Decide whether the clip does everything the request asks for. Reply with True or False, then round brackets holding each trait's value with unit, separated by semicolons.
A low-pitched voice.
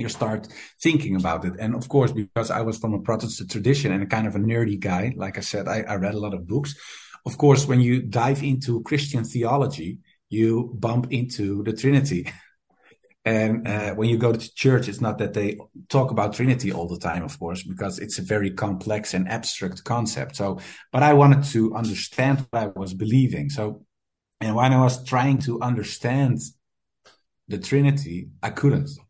True (115 Hz)